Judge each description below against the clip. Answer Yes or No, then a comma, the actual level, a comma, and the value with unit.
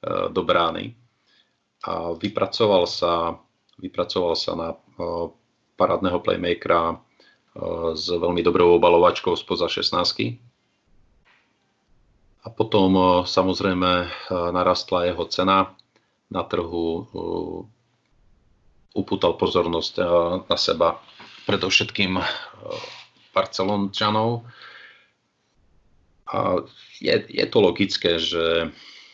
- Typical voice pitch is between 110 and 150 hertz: No, very low, 95 Hz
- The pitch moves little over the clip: No, average, 4.2 semitones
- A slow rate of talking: Yes, slow, 80 wpm